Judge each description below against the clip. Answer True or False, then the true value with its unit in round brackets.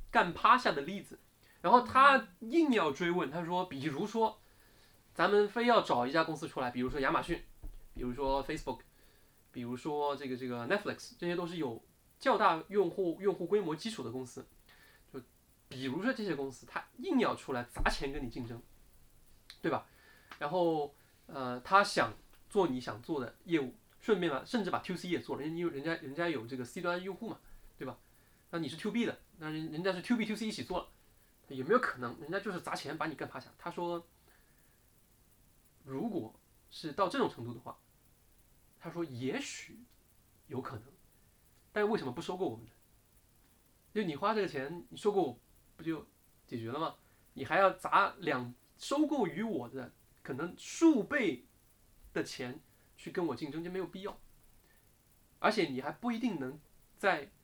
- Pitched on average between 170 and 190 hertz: False (160 Hz)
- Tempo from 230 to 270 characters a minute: True (265 characters per minute)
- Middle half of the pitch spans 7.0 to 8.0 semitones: True (7.4 semitones)